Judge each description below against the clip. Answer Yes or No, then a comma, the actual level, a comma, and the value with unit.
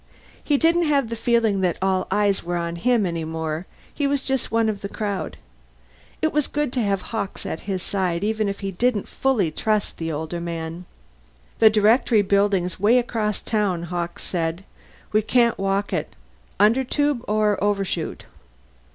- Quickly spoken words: No, average, 170 wpm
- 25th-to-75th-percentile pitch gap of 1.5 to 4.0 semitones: No, average, 4.4 semitones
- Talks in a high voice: Yes, high, 205 Hz